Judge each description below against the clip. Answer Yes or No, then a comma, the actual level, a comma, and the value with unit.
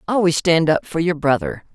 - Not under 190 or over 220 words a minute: Yes, fast, 205 wpm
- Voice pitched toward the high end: No, medium, 160 Hz